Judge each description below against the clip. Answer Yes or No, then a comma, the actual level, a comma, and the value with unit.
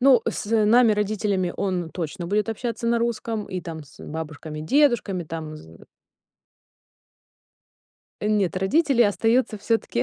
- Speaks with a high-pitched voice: Yes, high, 205 Hz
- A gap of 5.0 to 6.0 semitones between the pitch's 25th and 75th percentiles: Yes, average, 5.3 semitones